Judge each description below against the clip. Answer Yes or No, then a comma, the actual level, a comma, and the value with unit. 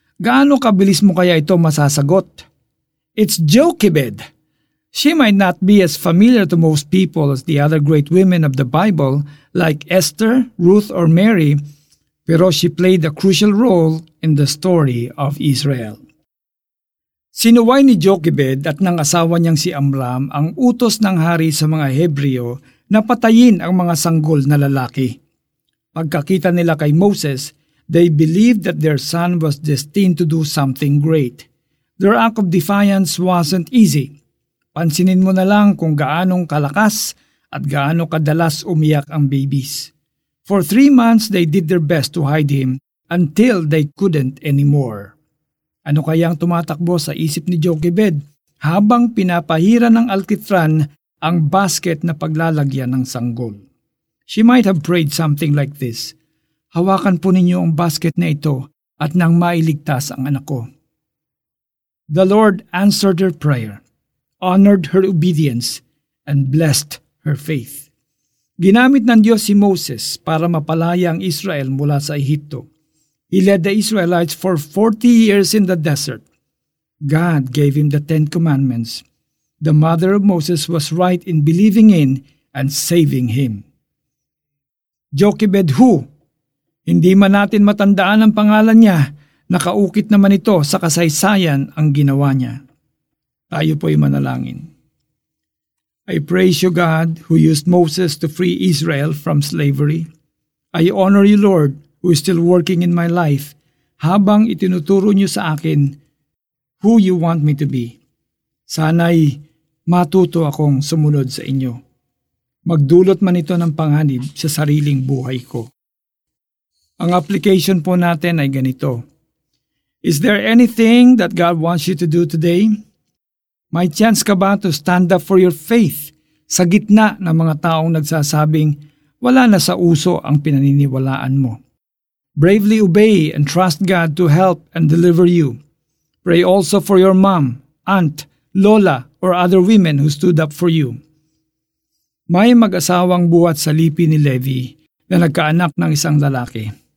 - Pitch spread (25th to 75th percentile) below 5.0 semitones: Yes, average, 4.2 semitones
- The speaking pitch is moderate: Yes, medium, 165 Hz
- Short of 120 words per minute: No, average, 140 wpm